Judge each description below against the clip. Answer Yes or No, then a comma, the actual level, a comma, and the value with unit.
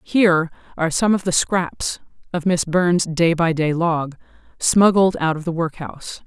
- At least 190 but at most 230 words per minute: No, average, 170 wpm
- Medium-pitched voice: Yes, medium, 170 Hz